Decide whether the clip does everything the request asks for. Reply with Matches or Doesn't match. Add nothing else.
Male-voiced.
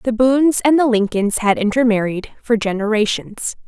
Doesn't match